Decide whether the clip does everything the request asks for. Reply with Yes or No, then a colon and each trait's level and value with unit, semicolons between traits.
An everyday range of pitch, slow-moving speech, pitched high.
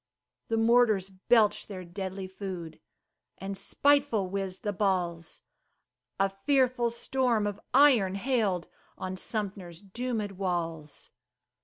Yes: average, 3.9 semitones; slow, 110 wpm; high, 195 Hz